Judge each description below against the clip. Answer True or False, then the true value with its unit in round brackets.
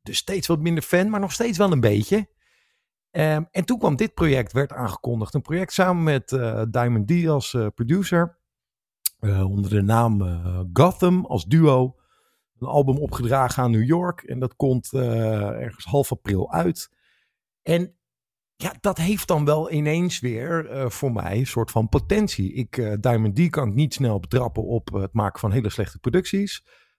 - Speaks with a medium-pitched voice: False (130 Hz)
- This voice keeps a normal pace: True (185 wpm)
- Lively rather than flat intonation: True (7.1 semitones)